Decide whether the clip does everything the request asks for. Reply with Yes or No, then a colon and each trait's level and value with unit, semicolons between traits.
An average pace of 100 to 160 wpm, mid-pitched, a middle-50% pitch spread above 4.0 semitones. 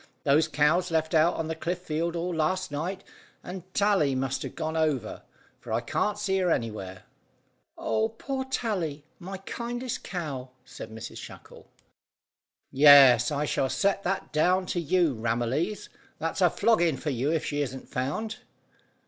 Yes: average, 155 wpm; medium, 160 Hz; average, 5.2 semitones